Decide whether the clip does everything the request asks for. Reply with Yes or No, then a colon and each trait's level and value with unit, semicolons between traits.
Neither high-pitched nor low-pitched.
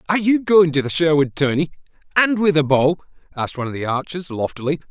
Yes: medium, 160 Hz